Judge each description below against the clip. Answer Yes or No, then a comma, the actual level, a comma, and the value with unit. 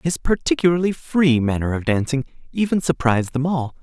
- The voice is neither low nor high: Yes, medium, 150 Hz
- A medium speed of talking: Yes, average, 155 wpm